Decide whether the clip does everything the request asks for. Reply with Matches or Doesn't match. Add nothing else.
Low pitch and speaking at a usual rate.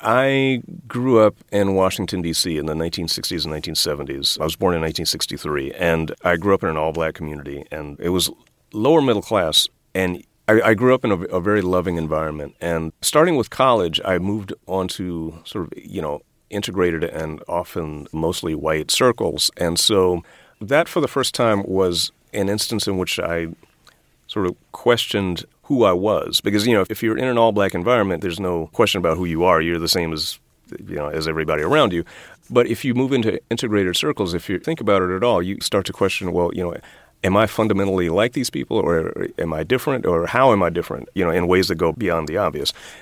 Doesn't match